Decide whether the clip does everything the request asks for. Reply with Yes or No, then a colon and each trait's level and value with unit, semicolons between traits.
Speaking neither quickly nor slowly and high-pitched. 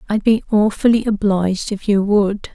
Yes: average, 165 wpm; high, 205 Hz